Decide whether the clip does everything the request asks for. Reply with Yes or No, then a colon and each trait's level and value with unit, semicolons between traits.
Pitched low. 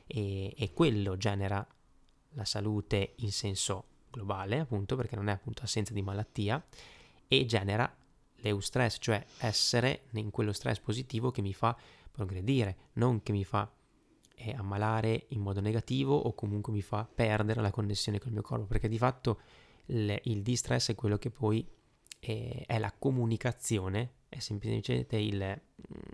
Yes: low, 110 Hz